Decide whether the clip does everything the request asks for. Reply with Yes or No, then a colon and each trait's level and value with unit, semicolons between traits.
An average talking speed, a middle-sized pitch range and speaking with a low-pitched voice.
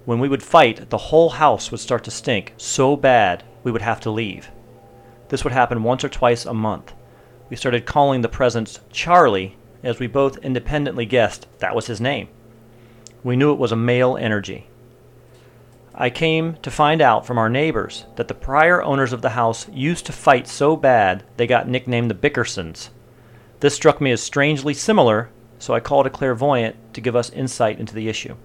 Yes: average, 190 wpm; average, 3.3 semitones; low, 120 Hz